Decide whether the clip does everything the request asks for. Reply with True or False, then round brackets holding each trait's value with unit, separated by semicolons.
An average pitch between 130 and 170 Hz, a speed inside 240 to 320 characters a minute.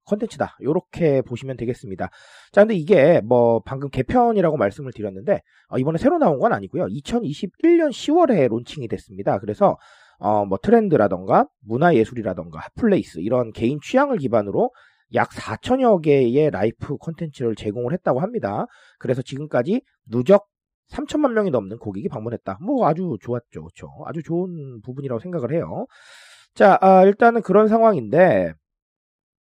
False (140 Hz; 345 characters per minute)